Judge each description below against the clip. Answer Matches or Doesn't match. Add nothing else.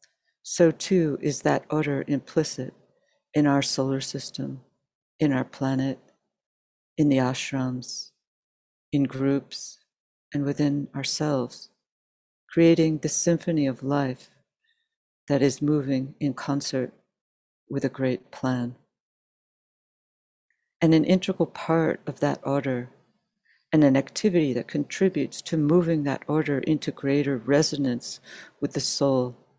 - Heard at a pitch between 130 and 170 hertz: Matches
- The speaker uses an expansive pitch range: Doesn't match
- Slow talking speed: Matches